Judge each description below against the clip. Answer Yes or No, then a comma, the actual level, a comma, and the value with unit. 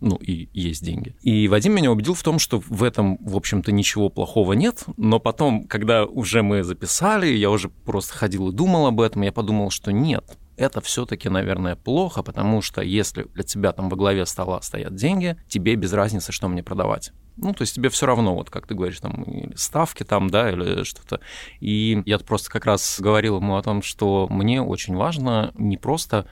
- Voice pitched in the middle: No, low, 105 Hz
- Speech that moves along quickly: Yes, fast, 205 wpm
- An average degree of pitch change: Yes, average, 3.2 semitones